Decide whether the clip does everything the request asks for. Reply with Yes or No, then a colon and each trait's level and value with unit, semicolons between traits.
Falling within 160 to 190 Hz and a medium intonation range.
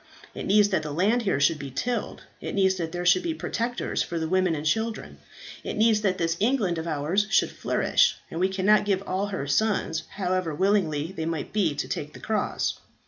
Yes: medium, 185 Hz; average, 4.4 semitones